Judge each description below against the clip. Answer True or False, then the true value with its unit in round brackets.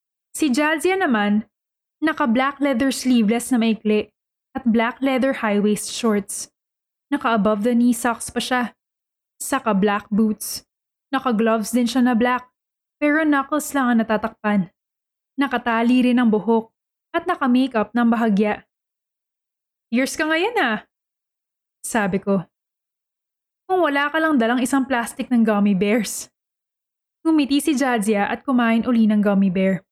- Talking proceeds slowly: False (140 wpm)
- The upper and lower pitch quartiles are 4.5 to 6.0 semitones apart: False (4.0 semitones)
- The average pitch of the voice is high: True (245 Hz)